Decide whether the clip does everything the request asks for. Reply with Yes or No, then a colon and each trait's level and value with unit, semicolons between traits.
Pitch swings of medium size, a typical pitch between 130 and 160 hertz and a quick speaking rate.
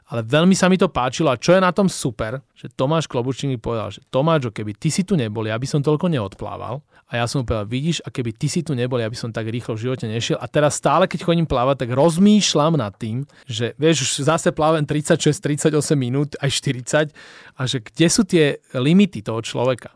Yes: average, 4.7 semitones; medium, 140 Hz; fast, 230 wpm